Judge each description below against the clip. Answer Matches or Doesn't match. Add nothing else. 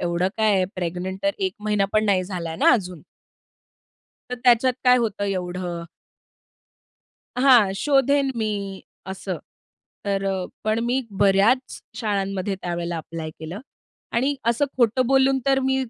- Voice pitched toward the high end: Matches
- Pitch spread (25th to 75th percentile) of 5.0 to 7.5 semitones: Matches